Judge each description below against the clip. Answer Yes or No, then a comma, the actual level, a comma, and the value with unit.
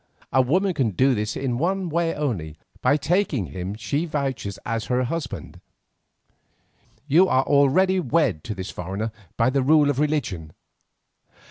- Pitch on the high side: No, low, 135 Hz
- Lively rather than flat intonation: Yes, wide, 6.1 semitones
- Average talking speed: Yes, average, 150 wpm